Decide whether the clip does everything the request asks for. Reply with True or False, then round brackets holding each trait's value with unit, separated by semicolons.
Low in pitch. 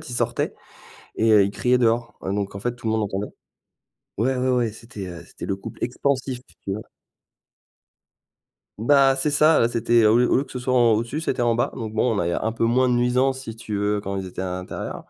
True (115 Hz)